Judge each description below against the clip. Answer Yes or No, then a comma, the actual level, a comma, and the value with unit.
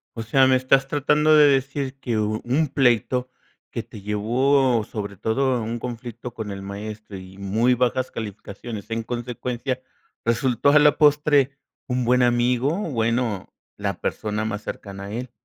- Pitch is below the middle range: Yes, low, 120 Hz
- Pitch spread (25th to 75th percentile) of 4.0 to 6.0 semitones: No, average, 3.5 semitones